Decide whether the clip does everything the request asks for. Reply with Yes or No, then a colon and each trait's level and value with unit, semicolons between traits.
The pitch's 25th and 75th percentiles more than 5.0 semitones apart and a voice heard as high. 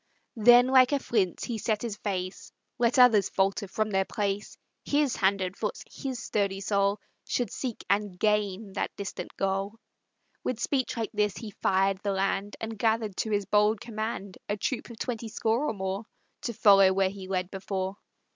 No: average, 2.7 semitones; high, 205 Hz